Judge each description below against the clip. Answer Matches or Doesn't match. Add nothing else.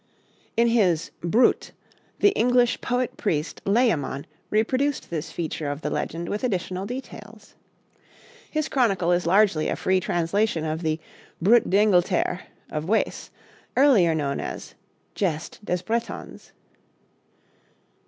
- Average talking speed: Doesn't match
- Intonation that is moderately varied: Doesn't match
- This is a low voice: Doesn't match